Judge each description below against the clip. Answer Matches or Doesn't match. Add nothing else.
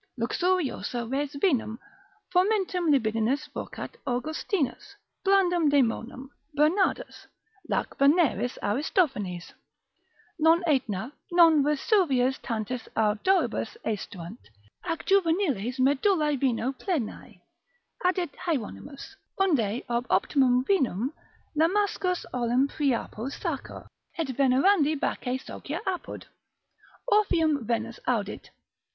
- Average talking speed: Doesn't match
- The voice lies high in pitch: Matches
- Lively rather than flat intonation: Matches